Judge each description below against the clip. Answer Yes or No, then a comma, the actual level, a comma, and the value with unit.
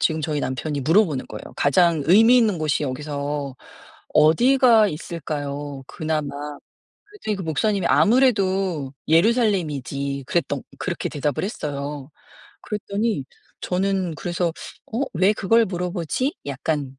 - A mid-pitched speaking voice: Yes, medium, 165 Hz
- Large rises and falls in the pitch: Yes, wide, 5.7 semitones